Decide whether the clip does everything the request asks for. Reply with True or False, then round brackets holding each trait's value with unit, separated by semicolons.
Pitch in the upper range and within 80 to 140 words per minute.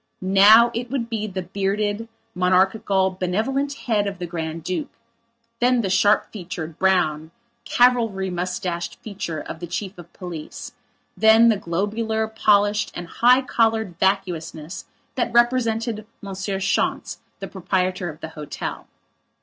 True (195 Hz; 135 wpm)